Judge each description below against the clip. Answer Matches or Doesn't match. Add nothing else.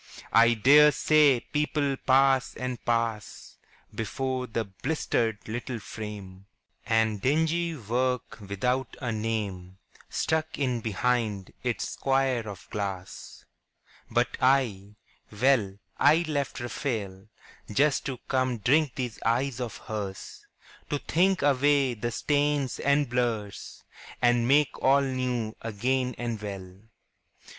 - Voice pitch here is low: Matches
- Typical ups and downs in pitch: Matches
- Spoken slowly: Matches